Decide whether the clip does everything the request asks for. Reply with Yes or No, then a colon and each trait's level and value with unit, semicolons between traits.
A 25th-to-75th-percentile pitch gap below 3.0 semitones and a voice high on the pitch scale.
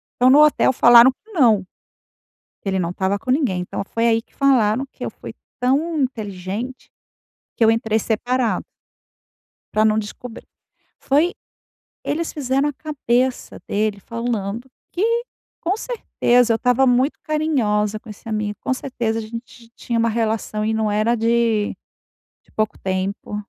No: average, 3.5 semitones; high, 230 Hz